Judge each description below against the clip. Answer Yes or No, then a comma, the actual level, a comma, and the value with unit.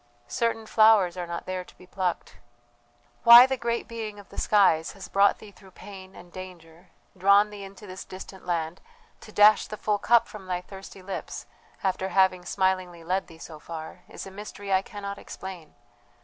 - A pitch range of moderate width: No, narrow, 2.3 semitones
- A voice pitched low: No, high, 190 Hz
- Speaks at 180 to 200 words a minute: Yes, average, 185 wpm